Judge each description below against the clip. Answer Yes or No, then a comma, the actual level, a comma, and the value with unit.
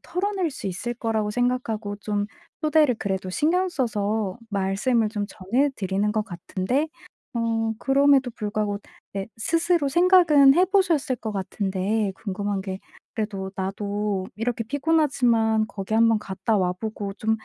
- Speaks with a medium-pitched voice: No, high, 220 Hz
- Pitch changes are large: No, average, 5.0 semitones